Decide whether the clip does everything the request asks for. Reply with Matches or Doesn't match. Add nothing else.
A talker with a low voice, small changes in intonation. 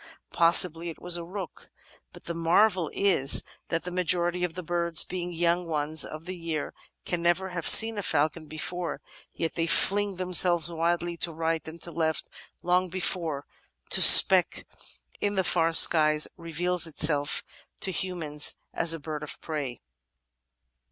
Doesn't match